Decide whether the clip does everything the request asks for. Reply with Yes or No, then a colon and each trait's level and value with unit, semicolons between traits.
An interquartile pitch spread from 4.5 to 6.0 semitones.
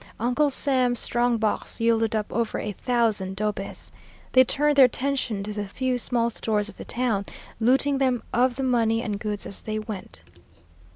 No: average, 3.1 semitones